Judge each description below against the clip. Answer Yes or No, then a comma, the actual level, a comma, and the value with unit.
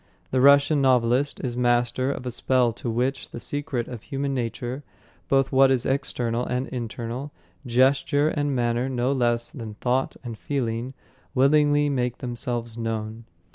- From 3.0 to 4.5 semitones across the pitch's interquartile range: No, narrow, 2.4 semitones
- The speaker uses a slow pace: No, average, 150 wpm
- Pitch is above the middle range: No, low, 125 Hz